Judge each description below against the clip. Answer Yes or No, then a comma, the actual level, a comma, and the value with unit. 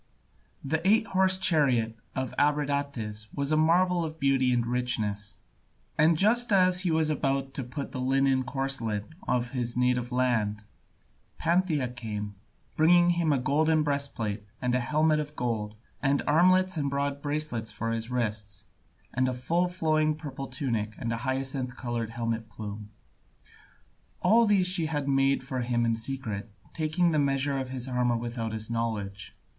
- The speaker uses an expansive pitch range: No, average, 4.8 semitones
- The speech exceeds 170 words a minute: No, average, 160 wpm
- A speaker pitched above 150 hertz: No, low, 135 Hz